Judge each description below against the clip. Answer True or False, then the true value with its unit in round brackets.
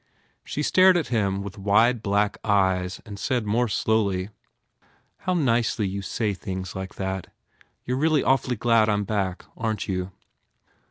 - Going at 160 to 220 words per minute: True (165 wpm)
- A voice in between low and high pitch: False (105 Hz)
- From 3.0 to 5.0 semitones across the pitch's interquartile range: True (3.8 semitones)